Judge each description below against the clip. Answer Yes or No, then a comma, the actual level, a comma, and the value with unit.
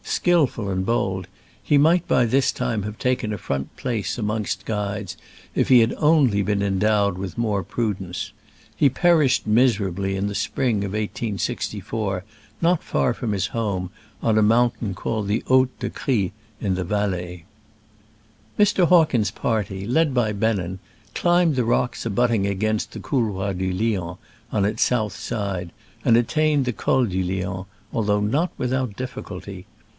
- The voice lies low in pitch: Yes, low, 105 Hz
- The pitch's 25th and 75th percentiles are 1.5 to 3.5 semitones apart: No, average, 4.2 semitones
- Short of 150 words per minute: No, average, 155 wpm